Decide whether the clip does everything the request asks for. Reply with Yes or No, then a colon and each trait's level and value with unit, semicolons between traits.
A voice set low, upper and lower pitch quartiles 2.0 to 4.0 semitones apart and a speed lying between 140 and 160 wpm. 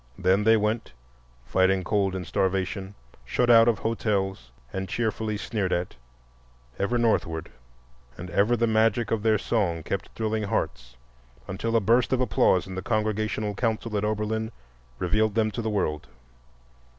Yes: low, 105 Hz; average, 2.9 semitones; average, 150 wpm